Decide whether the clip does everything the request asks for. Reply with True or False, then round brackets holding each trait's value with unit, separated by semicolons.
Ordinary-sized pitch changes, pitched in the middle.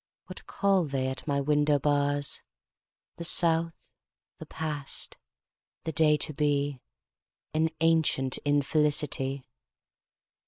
False (2.2 semitones; 145 Hz)